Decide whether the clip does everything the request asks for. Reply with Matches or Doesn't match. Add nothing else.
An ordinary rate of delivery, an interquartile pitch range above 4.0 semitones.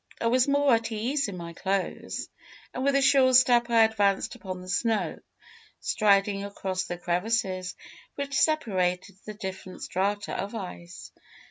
Matches